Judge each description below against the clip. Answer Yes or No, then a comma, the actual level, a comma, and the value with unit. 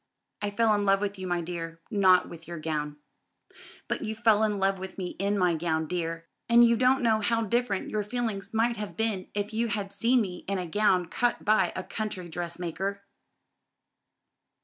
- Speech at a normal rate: Yes, average, 195 wpm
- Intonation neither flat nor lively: Yes, average, 3.7 semitones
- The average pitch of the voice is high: Yes, high, 200 Hz